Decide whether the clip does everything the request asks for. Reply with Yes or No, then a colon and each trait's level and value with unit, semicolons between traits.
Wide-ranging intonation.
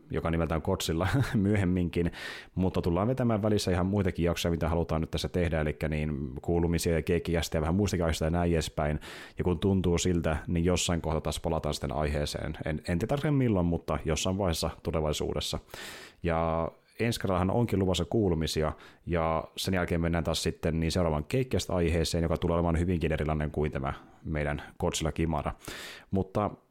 No: narrow, 2.4 semitones